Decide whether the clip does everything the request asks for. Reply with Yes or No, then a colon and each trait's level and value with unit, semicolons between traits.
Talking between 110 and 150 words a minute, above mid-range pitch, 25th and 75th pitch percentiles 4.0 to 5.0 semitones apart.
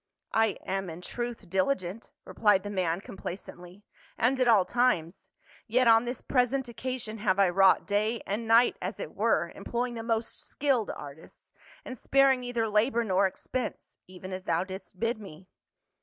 No: average, 185 wpm; high, 215 Hz; average, 4.3 semitones